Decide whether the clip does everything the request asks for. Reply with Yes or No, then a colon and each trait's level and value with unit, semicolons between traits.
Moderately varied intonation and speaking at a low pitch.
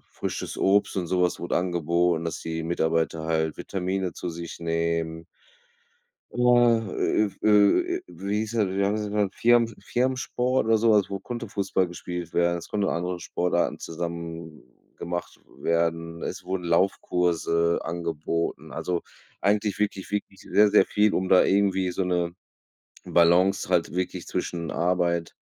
Yes: average, 3.3 semitones; very low, 90 Hz